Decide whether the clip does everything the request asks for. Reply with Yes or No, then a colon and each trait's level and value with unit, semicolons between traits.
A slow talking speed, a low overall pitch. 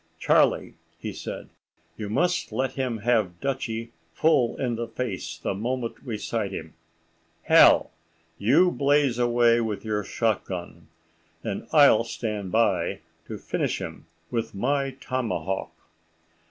Yes: slow, 125 wpm; low, 115 Hz